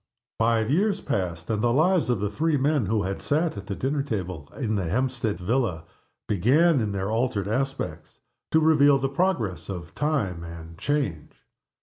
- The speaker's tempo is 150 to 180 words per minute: Yes, average, 170 wpm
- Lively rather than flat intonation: Yes, wide, 6.9 semitones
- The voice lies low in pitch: Yes, low, 115 Hz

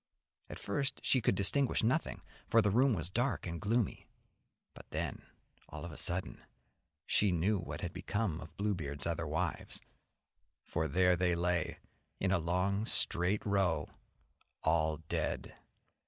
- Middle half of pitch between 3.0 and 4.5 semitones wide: Yes, average, 3.7 semitones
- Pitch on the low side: Yes, very low, 90 Hz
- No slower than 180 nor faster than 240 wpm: No, average, 145 wpm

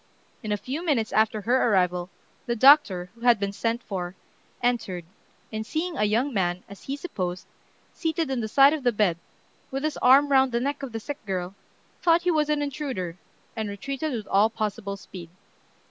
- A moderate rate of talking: Yes, average, 190 wpm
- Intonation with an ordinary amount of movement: No, wide, 5.9 semitones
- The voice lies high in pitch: Yes, high, 235 Hz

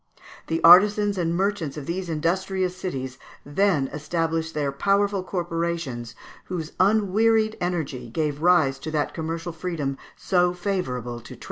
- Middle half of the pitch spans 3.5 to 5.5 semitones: Yes, average, 4.1 semitones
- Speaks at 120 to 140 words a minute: Yes, slow, 135 wpm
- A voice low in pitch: No, medium, 170 Hz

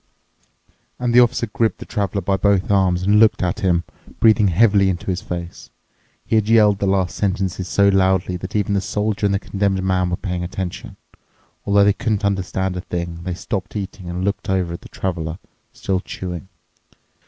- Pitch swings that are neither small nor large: No, narrow, 2.1 semitones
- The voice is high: No, very low, 95 Hz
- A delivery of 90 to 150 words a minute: No, average, 190 wpm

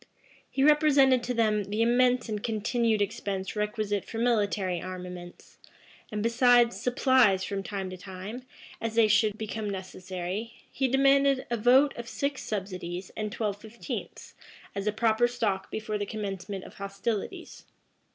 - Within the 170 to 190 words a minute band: No, average, 145 wpm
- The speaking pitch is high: Yes, high, 215 Hz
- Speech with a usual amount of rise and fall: Yes, average, 3.5 semitones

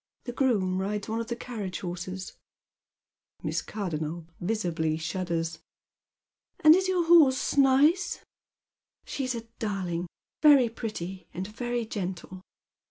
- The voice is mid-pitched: No, high, 210 Hz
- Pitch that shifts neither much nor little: No, wide, 5.9 semitones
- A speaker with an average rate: No, slow, 130 wpm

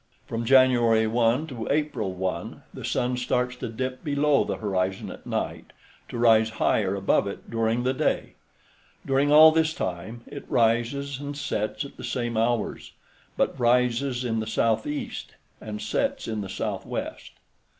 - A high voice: No, low, 120 Hz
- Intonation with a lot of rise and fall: No, average, 3.4 semitones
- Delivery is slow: No, average, 155 wpm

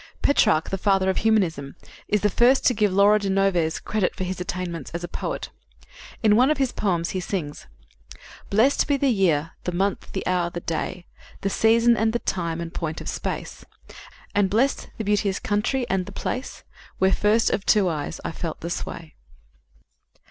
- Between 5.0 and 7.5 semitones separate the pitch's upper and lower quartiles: No, average, 3.9 semitones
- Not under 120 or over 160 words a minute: No, average, 185 wpm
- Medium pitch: No, high, 195 Hz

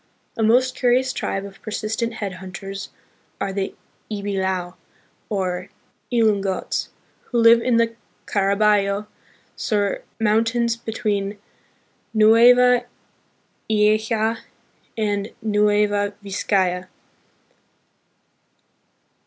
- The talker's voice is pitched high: Yes, high, 210 Hz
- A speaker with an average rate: No, slow, 80 wpm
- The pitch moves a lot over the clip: No, narrow, 2.4 semitones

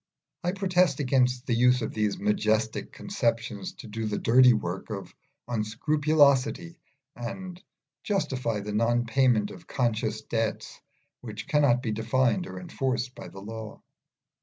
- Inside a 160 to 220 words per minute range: No, slow, 135 wpm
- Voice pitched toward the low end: Yes, low, 120 Hz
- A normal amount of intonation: Yes, average, 4.4 semitones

